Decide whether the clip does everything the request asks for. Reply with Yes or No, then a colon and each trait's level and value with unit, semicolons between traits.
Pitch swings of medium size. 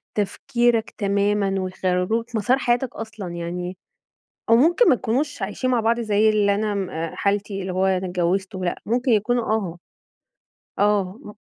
Yes: average, 3.6 semitones